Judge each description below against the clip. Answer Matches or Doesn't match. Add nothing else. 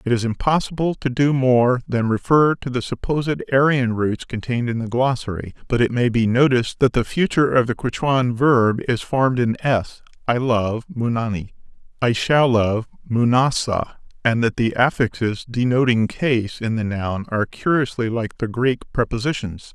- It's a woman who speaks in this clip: Doesn't match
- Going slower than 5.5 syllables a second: Matches